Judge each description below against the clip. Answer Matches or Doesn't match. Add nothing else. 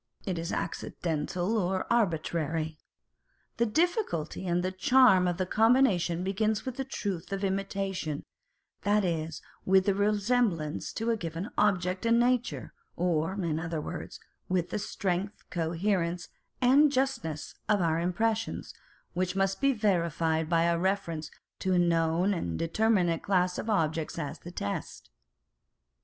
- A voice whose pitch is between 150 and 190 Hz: Matches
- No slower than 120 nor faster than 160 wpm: Matches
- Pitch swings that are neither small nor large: Matches